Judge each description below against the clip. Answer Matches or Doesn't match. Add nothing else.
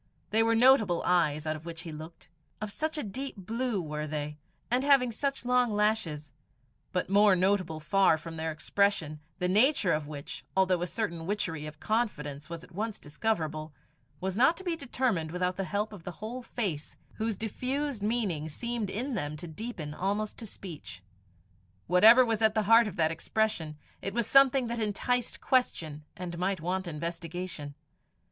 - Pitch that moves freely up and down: Matches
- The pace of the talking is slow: Doesn't match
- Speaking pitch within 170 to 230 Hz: Matches